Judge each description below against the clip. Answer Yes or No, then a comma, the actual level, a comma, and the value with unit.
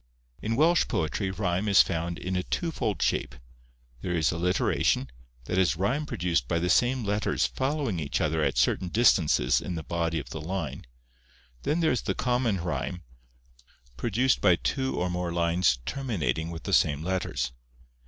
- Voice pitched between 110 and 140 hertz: No, very low, 90 Hz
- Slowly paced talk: No, average, 165 wpm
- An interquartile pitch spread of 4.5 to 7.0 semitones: Yes, wide, 5.5 semitones